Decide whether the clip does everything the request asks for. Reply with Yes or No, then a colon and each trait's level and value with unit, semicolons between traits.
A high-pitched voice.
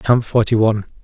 No: low, 110 Hz